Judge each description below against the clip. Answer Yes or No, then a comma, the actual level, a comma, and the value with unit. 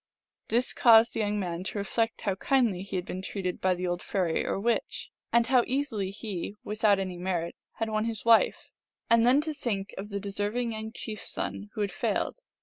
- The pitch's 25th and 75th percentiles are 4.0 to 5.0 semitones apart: No, average, 3.3 semitones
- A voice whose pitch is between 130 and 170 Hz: No, high, 210 Hz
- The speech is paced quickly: Yes, fast, 210 wpm